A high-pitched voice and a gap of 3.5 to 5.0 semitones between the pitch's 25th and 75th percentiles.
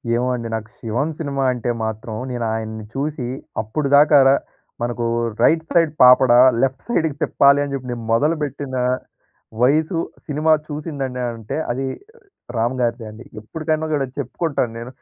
No: low, 135 Hz; average, 3.9 semitones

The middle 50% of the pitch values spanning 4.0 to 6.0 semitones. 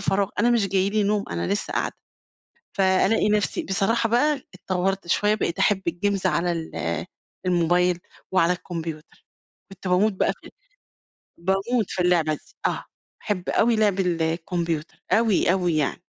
No: average, 3.2 semitones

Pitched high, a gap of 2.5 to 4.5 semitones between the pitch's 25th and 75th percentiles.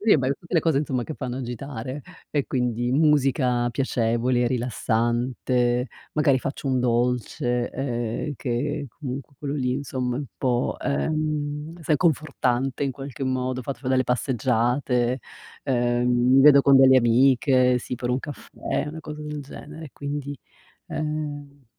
No: low, 130 Hz; average, 2.8 semitones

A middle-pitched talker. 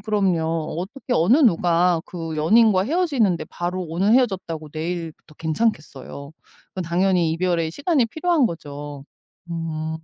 Yes: medium, 175 Hz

